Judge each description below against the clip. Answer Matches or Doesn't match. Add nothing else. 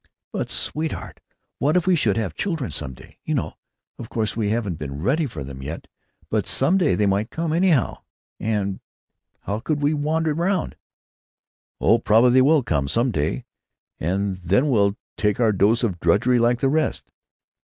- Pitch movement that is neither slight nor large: Doesn't match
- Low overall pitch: Matches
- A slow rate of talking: Doesn't match